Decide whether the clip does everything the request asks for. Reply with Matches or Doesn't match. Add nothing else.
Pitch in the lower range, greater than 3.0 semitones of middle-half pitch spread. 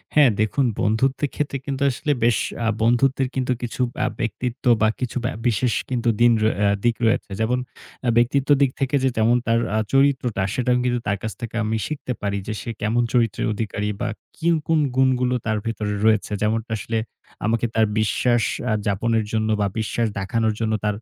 Doesn't match